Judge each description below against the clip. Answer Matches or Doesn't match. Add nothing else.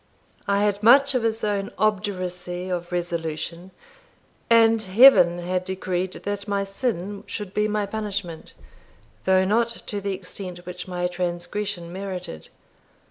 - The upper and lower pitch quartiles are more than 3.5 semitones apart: Doesn't match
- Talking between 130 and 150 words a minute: Matches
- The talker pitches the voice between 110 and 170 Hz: Doesn't match